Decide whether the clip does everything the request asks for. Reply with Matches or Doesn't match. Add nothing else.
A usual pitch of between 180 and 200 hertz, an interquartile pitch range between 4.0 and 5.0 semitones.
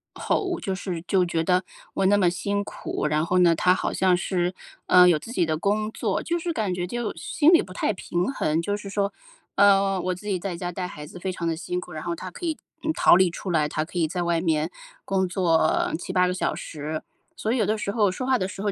Doesn't match